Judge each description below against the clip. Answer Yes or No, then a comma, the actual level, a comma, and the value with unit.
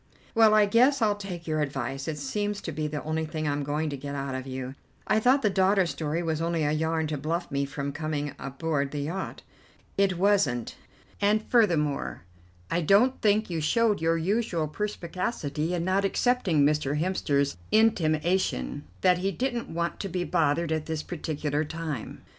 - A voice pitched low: No, medium, 160 Hz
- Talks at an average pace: Yes, average, 180 wpm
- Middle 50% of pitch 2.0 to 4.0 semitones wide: No, average, 4.9 semitones